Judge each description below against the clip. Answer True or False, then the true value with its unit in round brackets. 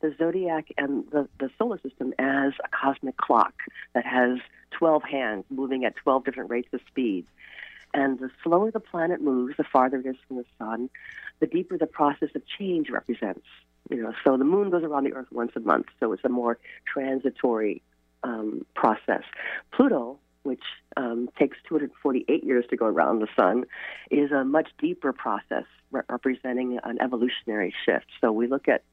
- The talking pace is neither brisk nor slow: True (180 wpm)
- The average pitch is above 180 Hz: False (135 Hz)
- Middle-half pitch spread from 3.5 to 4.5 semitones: True (3.8 semitones)